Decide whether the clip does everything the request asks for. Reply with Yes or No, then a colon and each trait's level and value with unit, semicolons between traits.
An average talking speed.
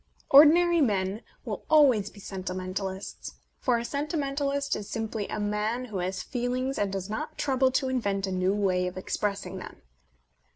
Yes: average, 160 wpm